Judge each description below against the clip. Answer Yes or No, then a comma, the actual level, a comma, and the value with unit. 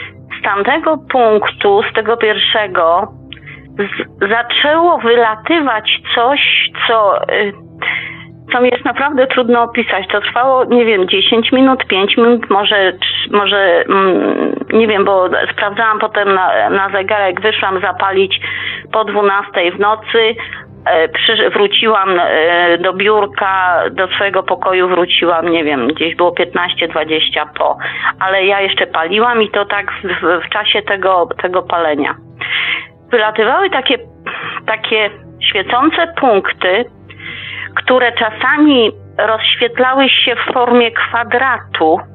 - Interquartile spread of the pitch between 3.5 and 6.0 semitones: Yes, average, 4.0 semitones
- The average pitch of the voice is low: No, high, 210 Hz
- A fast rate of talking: No, average, 115 wpm